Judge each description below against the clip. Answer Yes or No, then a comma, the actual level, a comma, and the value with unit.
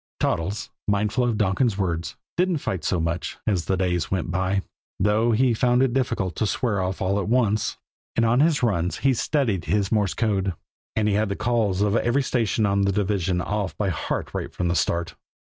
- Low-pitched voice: Yes, low, 100 Hz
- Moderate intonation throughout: Yes, average, 3.8 semitones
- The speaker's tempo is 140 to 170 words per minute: No, average, 200 wpm